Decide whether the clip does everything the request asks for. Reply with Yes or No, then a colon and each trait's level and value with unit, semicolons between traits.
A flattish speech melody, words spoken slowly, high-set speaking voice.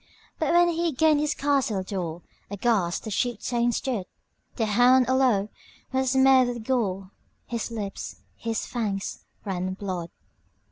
No: average, 4.9 semitones; slow, 125 wpm; high, 235 Hz